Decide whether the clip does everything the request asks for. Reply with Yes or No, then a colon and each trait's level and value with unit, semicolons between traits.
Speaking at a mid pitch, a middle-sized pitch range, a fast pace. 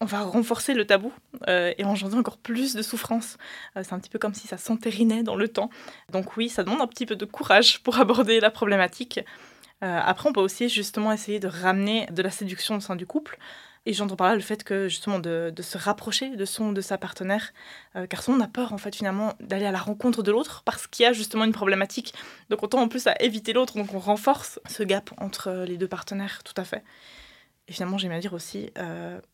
No: high, 210 Hz; average, 3.2 semitones; fast, 245 wpm